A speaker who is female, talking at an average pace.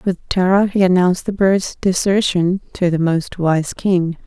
Yes: female; average, 170 wpm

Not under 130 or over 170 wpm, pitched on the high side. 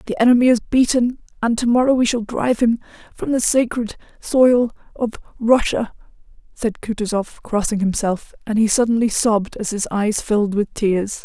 Yes: average, 160 wpm; high, 225 Hz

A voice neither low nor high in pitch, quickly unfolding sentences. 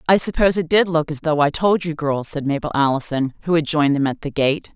Yes: medium, 155 Hz; fast, 265 wpm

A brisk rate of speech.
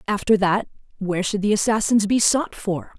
No: average, 180 wpm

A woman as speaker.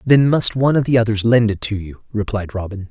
No: male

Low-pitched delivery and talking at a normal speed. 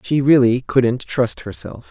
Yes: low, 125 Hz; average, 160 wpm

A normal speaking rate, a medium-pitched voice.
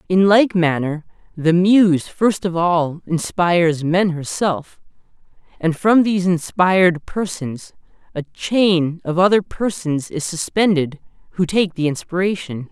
No: slow, 125 wpm; medium, 175 Hz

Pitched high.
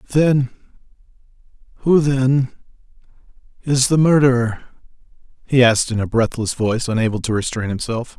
No: low, 125 Hz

